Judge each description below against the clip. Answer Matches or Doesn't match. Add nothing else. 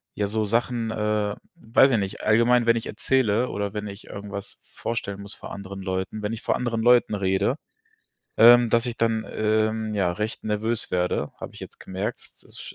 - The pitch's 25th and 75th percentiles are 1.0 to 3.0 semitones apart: Matches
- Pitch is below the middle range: Matches